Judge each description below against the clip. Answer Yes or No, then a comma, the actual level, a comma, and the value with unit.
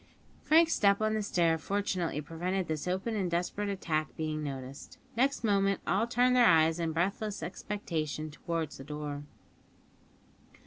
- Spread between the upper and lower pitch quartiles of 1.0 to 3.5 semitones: No, average, 4.7 semitones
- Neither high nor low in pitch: Yes, medium, 180 Hz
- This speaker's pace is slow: No, average, 145 wpm